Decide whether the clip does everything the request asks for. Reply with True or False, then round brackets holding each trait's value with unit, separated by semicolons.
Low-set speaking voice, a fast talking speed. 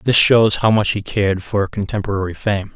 False (105 Hz; 195 wpm)